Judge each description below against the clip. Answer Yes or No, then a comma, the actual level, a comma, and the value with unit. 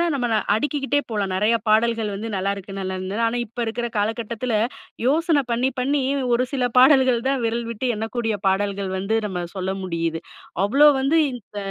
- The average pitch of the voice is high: Yes, high, 225 Hz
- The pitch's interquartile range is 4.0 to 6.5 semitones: Yes, average, 4.3 semitones